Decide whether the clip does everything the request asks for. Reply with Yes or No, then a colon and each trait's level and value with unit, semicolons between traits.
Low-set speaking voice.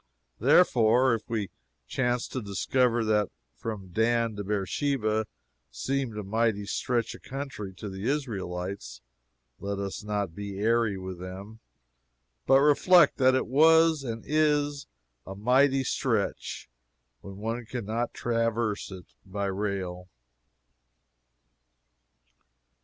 Yes: low, 110 Hz